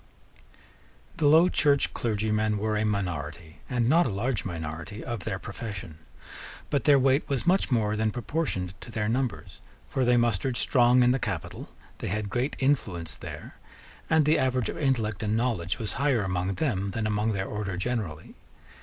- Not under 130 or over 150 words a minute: No, average, 170 wpm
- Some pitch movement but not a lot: Yes, average, 4.8 semitones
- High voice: No, low, 110 Hz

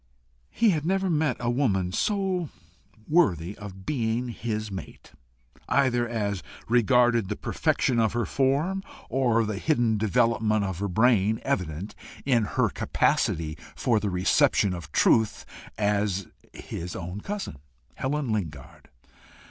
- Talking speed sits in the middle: No, slow, 125 wpm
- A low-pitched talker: Yes, low, 110 Hz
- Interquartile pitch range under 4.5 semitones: No, average, 5.0 semitones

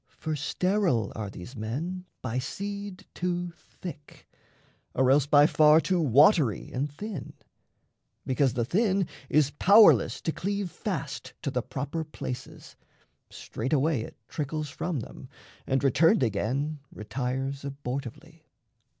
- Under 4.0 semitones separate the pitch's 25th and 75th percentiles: No, average, 5.0 semitones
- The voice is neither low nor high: Yes, medium, 145 Hz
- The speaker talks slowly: Yes, slow, 125 wpm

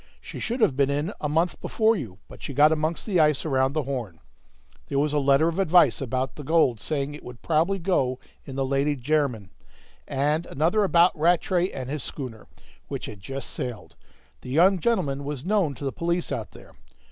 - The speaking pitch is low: No, medium, 150 Hz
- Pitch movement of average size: Yes, average, 4.0 semitones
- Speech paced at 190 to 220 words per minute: Yes, average, 200 wpm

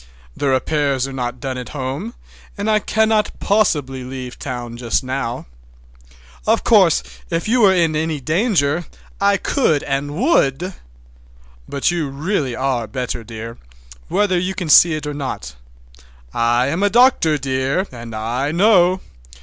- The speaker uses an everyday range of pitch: No, wide, 6.1 semitones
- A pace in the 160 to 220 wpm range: No, average, 150 wpm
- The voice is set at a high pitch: No, medium, 145 Hz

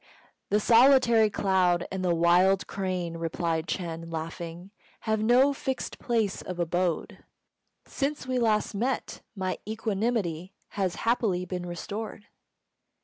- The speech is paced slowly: Yes, slow, 120 wpm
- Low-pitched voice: No, high, 190 Hz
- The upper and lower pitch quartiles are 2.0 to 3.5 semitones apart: No, average, 4.5 semitones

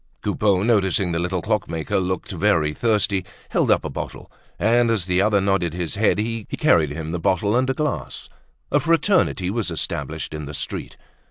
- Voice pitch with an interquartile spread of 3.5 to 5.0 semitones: Yes, average, 4.3 semitones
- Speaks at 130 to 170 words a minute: No, average, 180 wpm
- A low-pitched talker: Yes, very low, 95 Hz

